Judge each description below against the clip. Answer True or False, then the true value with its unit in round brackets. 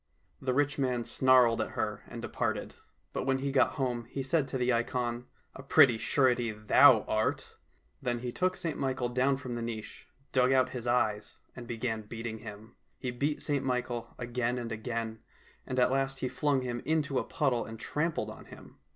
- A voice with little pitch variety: True (2.3 semitones)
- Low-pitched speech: True (125 Hz)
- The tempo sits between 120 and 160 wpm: False (200 wpm)